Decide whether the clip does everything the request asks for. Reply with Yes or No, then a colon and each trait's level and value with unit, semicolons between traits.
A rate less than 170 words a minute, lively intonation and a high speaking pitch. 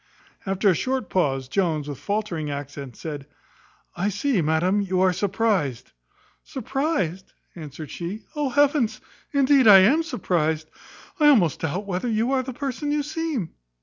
Yes: average, 150 wpm; wide, 8.5 semitones; high, 195 Hz